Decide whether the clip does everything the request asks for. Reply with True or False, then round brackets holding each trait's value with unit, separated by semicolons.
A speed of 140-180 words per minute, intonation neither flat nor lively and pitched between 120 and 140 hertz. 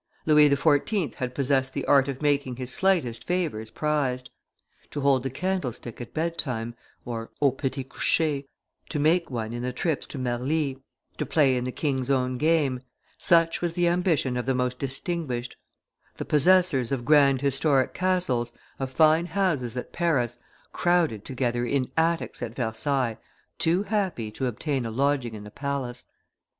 True (160 wpm; 4.2 semitones; 135 Hz)